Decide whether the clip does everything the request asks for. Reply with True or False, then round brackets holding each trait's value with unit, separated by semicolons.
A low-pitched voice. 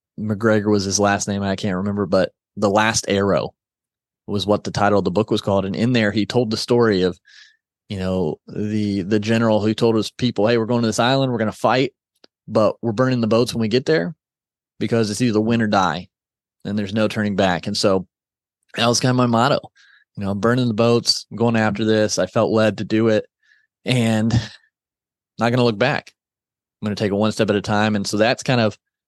True (110 Hz)